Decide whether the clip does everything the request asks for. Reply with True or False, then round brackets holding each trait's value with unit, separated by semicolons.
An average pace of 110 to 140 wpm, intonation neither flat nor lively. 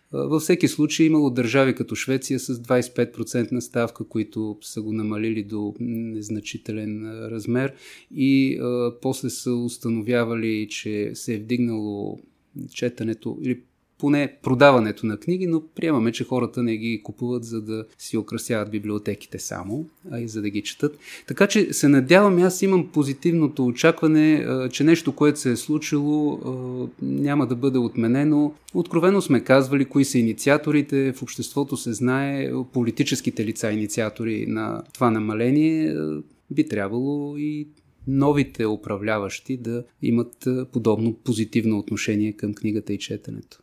True (135 wpm; 4.4 semitones)